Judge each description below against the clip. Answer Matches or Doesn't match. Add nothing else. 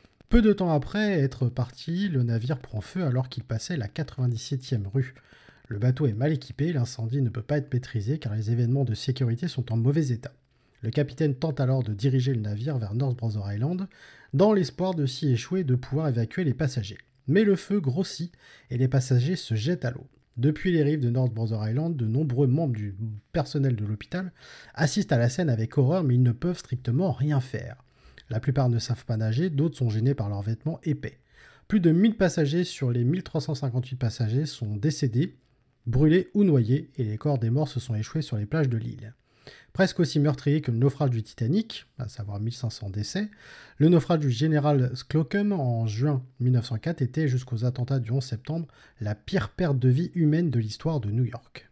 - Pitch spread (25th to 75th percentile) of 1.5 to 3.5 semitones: Doesn't match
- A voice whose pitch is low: Matches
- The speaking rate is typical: Matches